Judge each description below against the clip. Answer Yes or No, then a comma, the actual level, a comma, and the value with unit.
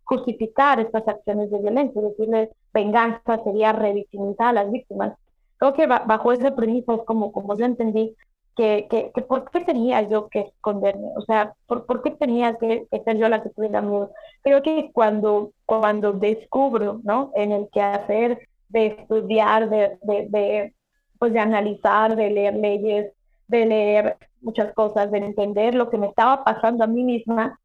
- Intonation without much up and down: Yes, narrow, 2.2 semitones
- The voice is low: No, high, 220 Hz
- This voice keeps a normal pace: Yes, average, 170 wpm